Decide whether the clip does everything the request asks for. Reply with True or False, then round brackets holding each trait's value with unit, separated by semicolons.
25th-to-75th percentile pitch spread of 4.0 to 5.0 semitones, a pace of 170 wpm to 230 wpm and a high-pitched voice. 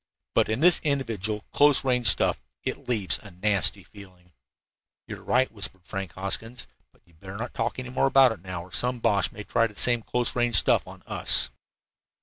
False (4.4 semitones; 195 wpm; 110 Hz)